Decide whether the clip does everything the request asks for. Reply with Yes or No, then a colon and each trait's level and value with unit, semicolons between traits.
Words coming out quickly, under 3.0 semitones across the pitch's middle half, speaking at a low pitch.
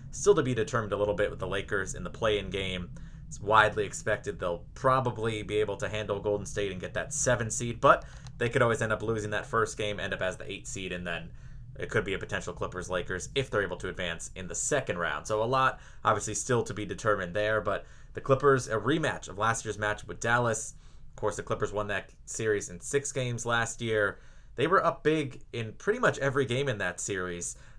No: fast, 235 wpm; average, 4.0 semitones; low, 110 Hz